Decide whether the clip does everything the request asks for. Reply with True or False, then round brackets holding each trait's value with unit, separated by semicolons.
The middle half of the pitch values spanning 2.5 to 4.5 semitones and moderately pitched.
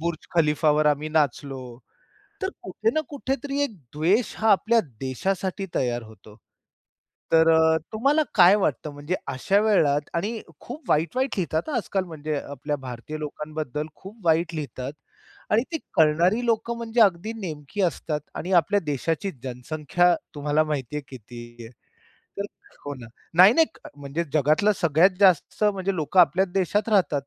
False (5.6 semitones; 165 Hz)